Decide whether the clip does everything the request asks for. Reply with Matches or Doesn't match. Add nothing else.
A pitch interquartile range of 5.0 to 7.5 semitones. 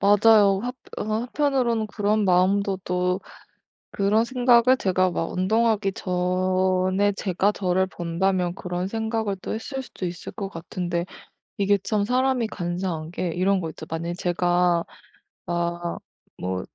Doesn't match